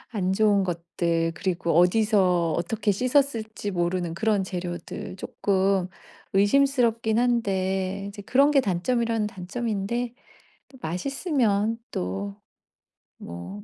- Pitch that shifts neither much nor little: Yes, average, 4.5 semitones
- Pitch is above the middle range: Yes, high, 200 Hz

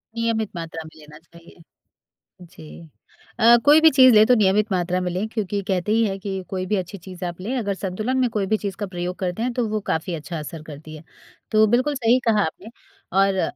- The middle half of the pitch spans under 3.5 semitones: No, average, 4.1 semitones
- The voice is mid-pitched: No, high, 195 Hz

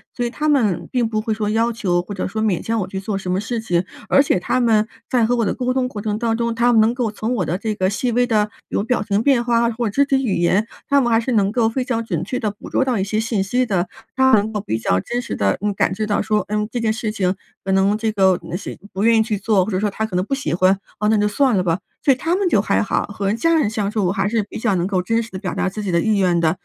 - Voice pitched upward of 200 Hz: Yes, high, 215 Hz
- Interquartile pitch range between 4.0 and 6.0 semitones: No, average, 3.4 semitones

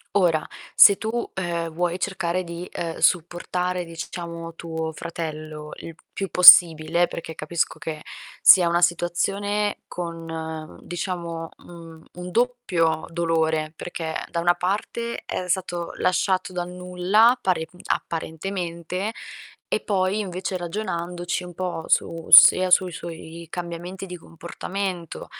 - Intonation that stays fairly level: Yes, narrow, 1.8 semitones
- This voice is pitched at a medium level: Yes, medium, 175 Hz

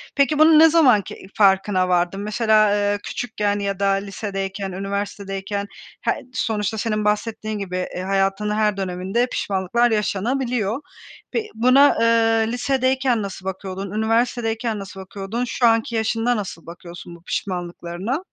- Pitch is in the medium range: No, high, 210 Hz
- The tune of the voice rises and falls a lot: No, average, 3.0 semitones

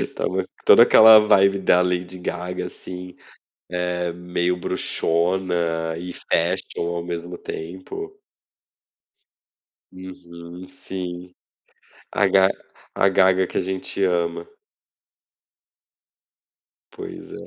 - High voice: No, very low, 90 Hz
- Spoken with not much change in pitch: Yes, narrow, 1.2 semitones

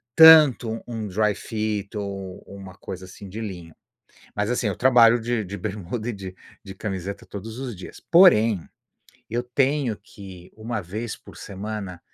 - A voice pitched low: Yes, low, 105 Hz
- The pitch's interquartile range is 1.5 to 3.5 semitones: Yes, average, 3.2 semitones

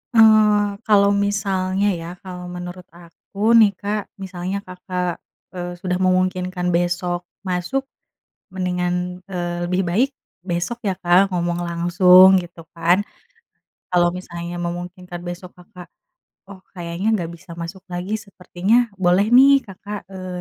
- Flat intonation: Yes, narrow, 1.5 semitones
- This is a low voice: No, medium, 180 Hz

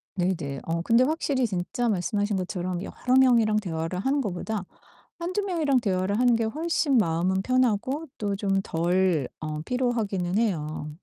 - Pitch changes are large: Yes, wide, 5.8 semitones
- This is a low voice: No, high, 205 Hz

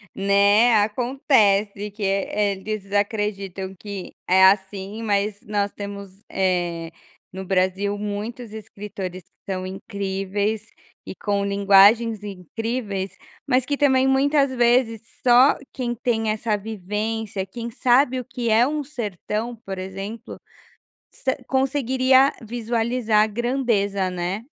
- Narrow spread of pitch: No, average, 3.4 semitones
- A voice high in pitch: Yes, high, 210 Hz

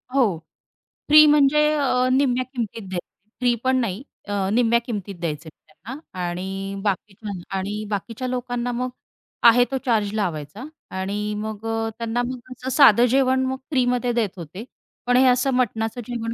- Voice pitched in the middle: No, high, 230 Hz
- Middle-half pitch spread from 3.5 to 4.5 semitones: Yes, average, 3.8 semitones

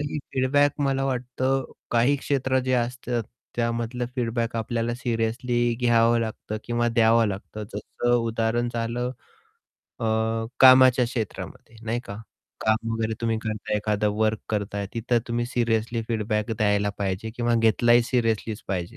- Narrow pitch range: Yes, narrow, 1.8 semitones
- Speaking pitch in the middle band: No, low, 115 Hz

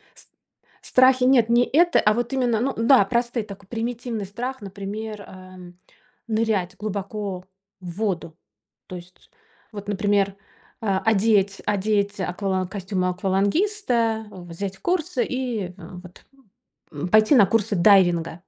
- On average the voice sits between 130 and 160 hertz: No, high, 205 Hz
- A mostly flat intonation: No, average, 3.6 semitones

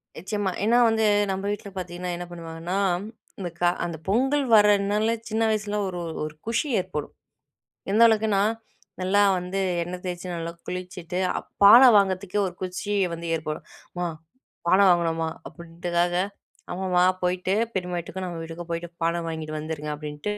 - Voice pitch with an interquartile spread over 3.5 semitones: No, average, 3.0 semitones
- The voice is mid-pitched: Yes, medium, 180 Hz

